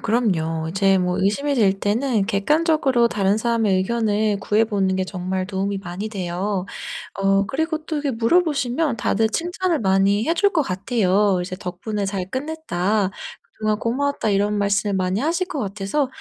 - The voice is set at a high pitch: Yes, high, 210 Hz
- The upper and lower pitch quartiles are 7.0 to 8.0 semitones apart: No, average, 5.2 semitones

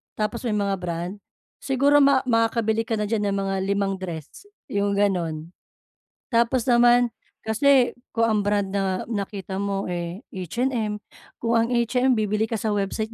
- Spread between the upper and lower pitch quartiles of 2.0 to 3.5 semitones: Yes, average, 3.2 semitones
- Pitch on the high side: Yes, high, 210 Hz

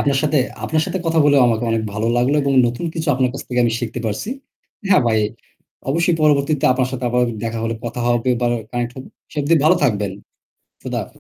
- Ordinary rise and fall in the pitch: Yes, average, 4.1 semitones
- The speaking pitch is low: Yes, low, 125 Hz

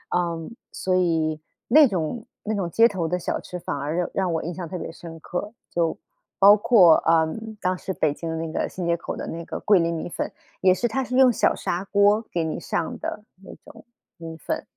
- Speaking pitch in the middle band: Yes, medium, 175 Hz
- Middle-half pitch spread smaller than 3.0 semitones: No, average, 3.6 semitones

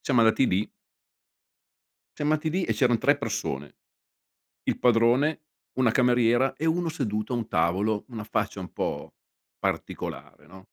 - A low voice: Yes, low, 120 Hz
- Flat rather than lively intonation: No, average, 4.3 semitones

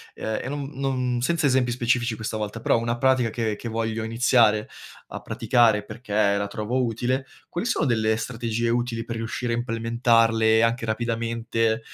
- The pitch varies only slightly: Yes, narrow, 1.6 semitones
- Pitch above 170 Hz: No, low, 115 Hz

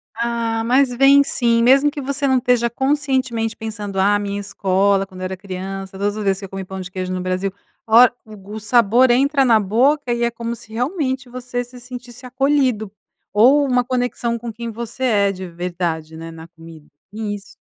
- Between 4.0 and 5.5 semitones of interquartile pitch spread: Yes, average, 4.4 semitones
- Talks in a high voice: Yes, high, 230 Hz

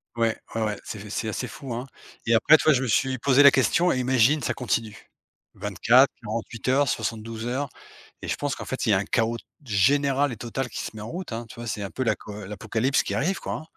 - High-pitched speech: No, low, 120 Hz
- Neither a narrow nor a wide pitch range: Yes, average, 3.5 semitones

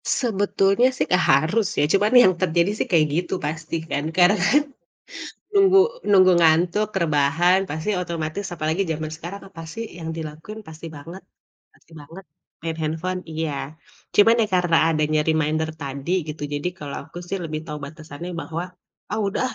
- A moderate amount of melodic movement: Yes, average, 3.5 semitones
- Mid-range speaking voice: Yes, medium, 170 Hz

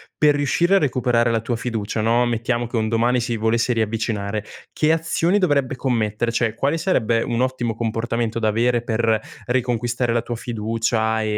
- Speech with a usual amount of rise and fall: No, narrow, 1.9 semitones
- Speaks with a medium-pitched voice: No, low, 120 Hz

